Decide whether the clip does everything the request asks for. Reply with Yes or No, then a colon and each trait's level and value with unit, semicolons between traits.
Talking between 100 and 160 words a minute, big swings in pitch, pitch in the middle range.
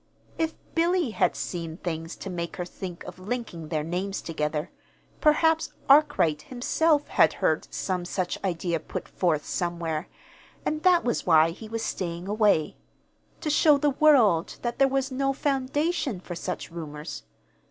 No: average, 150 wpm; wide, 8.6 semitones; high, 195 Hz